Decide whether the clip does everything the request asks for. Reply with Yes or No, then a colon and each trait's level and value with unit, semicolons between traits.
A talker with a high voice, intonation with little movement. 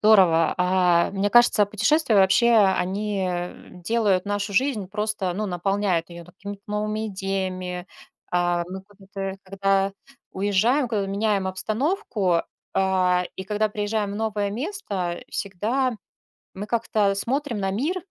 Yes: high, 200 Hz; narrow, 2.3 semitones